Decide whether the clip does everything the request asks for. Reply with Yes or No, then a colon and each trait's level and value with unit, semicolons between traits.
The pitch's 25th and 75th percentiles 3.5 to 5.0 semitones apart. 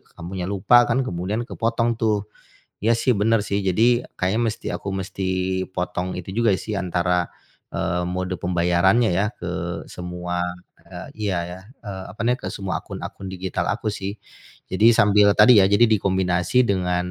No: average, 2.8 semitones